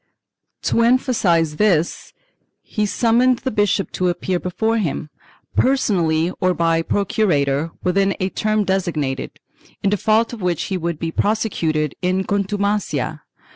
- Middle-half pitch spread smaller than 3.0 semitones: No, average, 4.4 semitones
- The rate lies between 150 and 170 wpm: No, slow, 135 wpm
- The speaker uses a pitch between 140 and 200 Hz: Yes, high, 190 Hz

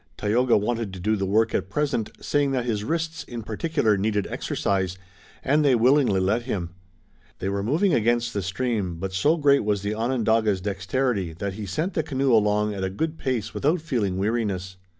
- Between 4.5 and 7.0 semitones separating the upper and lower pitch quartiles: Yes, average, 4.9 semitones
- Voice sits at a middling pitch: No, low, 110 Hz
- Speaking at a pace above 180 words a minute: Yes, average, 190 wpm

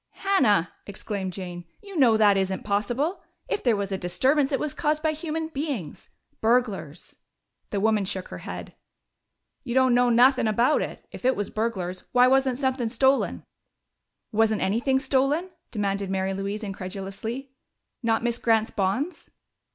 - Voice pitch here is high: Yes, high, 230 Hz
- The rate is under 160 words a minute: Yes, average, 150 wpm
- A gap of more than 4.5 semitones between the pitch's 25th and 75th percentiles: Yes, average, 5.2 semitones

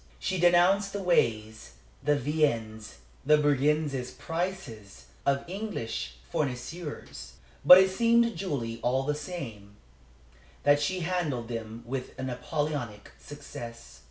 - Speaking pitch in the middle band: Yes, medium, 145 Hz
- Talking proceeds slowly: Yes, slow, 120 wpm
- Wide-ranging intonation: Yes, wide, 6.9 semitones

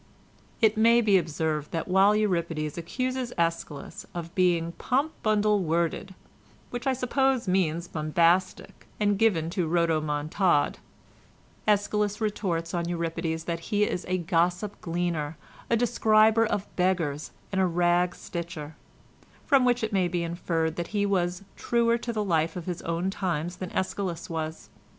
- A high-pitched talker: No, medium, 180 Hz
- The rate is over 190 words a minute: No, average, 145 wpm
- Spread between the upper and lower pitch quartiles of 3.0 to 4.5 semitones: Yes, average, 4.0 semitones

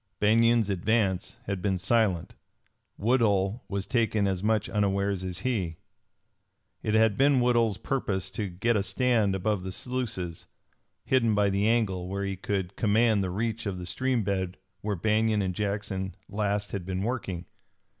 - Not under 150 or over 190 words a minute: Yes, average, 155 wpm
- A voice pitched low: Yes, low, 100 Hz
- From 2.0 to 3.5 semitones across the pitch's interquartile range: Yes, average, 2.9 semitones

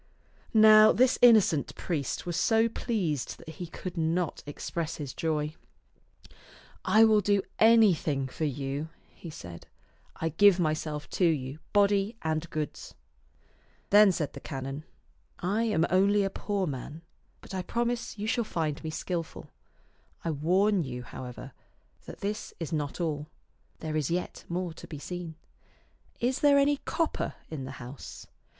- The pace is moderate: Yes, average, 155 wpm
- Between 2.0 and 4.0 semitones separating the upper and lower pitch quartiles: No, average, 5.3 semitones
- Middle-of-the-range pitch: Yes, medium, 170 Hz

